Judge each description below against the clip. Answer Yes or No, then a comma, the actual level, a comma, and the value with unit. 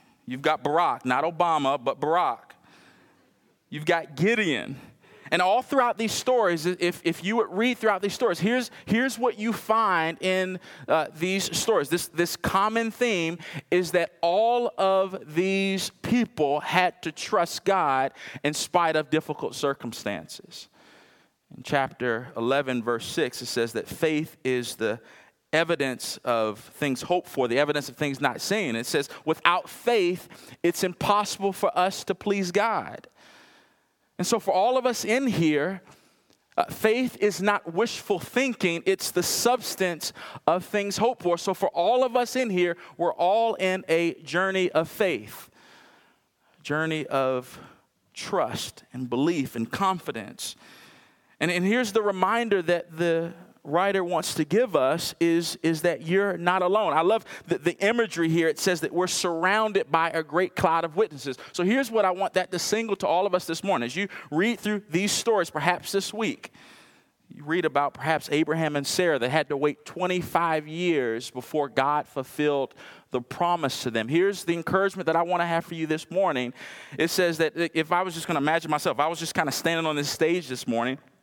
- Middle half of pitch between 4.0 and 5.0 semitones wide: Yes, average, 4.3 semitones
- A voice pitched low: No, medium, 175 Hz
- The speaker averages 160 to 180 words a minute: Yes, average, 175 wpm